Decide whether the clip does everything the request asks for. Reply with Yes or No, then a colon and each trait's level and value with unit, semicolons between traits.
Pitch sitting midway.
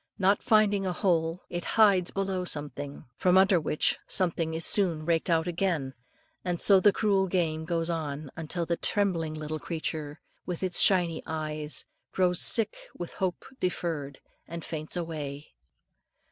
Yes: medium, 170 Hz